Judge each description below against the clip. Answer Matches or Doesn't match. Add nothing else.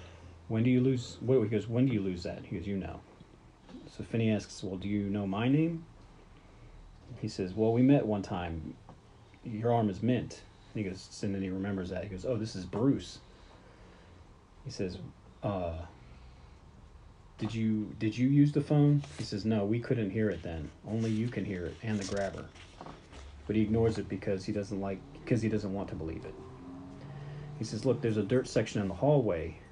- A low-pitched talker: Matches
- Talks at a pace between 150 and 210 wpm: Matches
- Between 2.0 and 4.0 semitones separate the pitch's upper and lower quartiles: Matches